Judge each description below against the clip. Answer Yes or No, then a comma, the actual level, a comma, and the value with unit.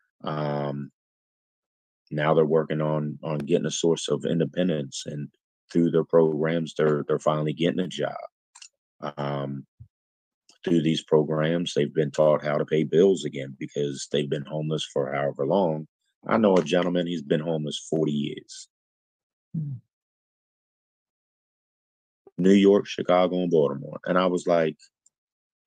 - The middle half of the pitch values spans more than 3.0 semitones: No, narrow, 2.6 semitones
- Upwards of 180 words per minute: No, slow, 135 wpm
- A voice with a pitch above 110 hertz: No, very low, 75 Hz